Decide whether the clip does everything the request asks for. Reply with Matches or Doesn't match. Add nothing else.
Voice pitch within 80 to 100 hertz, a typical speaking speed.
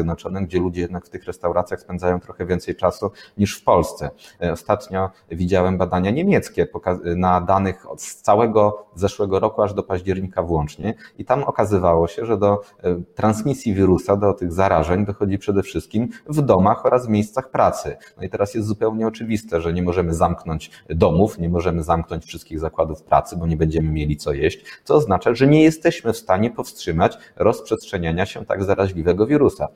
Doesn't match